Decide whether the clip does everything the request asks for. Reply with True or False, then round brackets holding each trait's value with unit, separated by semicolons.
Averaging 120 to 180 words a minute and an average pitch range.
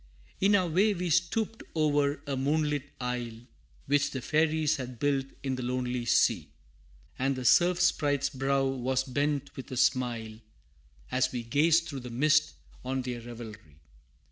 True (155 wpm; 3.5 semitones)